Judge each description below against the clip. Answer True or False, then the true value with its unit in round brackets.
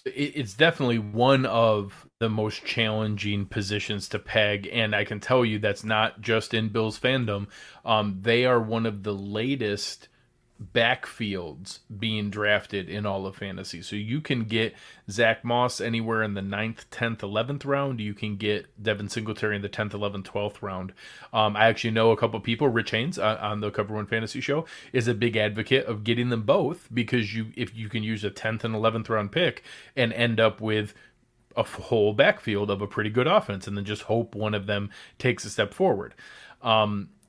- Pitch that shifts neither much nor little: False (2.0 semitones)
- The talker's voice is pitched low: True (110 Hz)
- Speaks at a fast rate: False (195 wpm)